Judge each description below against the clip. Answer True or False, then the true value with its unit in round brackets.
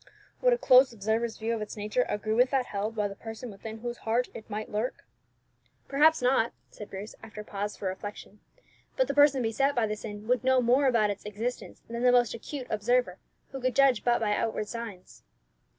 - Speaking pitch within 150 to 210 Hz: False (230 Hz)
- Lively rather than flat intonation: False (3.0 semitones)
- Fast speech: True (210 wpm)